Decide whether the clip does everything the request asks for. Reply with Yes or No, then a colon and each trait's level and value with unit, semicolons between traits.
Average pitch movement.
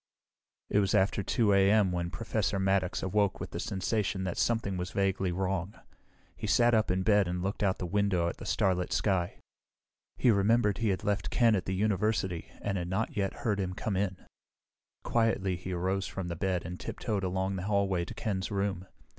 No: narrow, 2.0 semitones